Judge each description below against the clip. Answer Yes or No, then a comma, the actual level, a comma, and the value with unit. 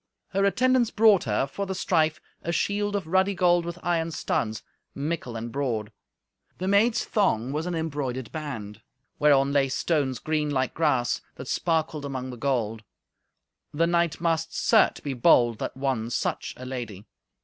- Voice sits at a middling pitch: Yes, medium, 150 Hz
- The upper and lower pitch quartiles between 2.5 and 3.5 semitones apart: No, average, 5.3 semitones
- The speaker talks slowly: No, average, 160 wpm